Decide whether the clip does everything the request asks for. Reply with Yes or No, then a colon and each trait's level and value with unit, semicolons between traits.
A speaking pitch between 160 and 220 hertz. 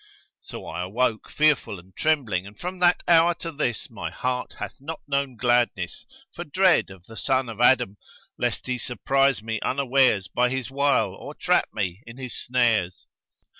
No: low, 125 Hz